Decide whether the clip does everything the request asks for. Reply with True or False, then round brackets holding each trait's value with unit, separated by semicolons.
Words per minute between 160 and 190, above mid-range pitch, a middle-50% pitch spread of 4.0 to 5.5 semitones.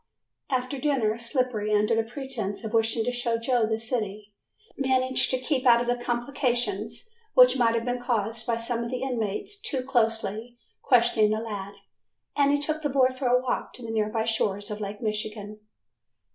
False (180 wpm; 235 Hz; 2.7 semitones)